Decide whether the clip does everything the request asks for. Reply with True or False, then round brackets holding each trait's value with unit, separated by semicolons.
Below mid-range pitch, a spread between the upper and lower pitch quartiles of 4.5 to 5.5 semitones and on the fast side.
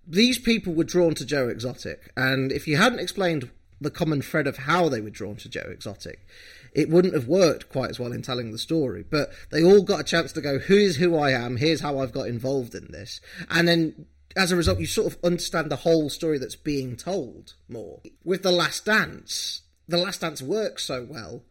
False (155 Hz; 4.9 semitones; 225 wpm)